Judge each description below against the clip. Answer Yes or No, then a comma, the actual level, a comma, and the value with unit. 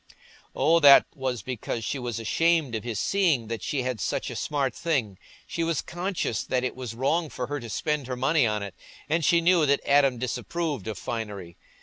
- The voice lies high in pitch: No, low, 130 Hz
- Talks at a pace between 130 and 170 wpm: No, average, 200 wpm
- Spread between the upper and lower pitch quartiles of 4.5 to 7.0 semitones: Yes, wide, 5.5 semitones